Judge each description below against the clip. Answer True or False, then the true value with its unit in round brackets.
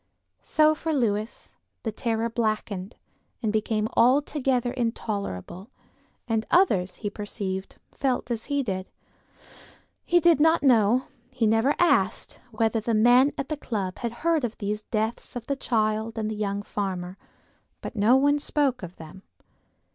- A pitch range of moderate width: True (4.1 semitones)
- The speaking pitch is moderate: False (225 Hz)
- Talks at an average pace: True (145 wpm)